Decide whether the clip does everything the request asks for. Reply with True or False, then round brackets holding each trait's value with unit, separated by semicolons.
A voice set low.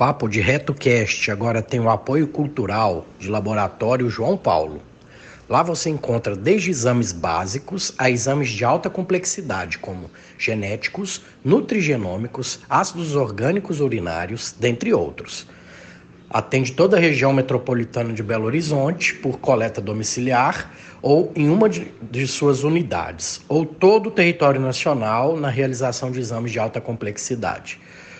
True (125 Hz)